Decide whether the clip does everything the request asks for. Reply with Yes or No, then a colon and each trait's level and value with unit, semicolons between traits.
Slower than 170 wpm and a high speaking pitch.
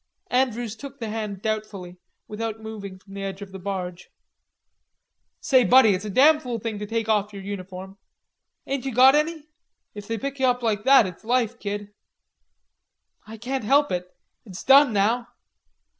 No: average, 175 wpm; high, 220 Hz